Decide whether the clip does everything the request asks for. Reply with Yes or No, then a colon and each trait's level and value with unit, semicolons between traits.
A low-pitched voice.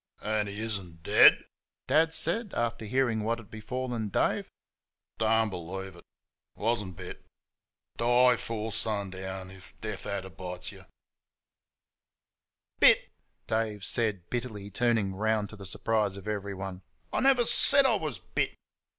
Yes: low, 110 Hz